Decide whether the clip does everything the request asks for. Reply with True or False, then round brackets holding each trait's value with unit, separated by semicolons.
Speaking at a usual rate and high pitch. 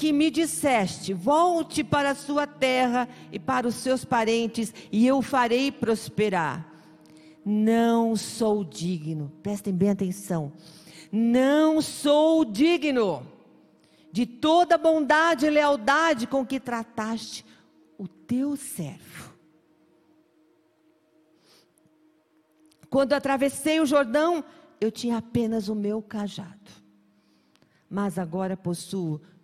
False (105 wpm; 225 Hz)